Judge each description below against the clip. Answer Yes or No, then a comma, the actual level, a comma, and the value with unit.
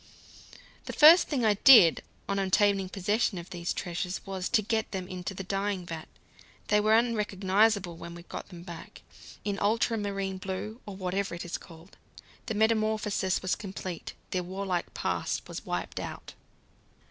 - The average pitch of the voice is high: Yes, high, 195 Hz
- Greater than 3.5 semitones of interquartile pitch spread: No, narrow, 2.6 semitones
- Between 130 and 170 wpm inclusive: Yes, average, 160 wpm